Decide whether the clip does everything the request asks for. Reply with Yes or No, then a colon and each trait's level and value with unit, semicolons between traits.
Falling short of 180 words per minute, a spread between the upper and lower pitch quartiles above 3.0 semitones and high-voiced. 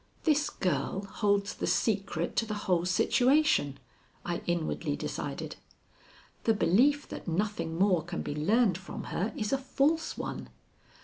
Yes: average, 140 wpm; wide, 5.6 semitones; high, 200 Hz